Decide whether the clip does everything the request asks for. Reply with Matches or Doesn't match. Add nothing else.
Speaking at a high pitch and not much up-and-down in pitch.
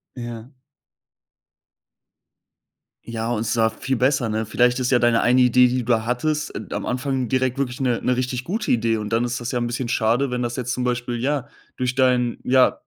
Doesn't match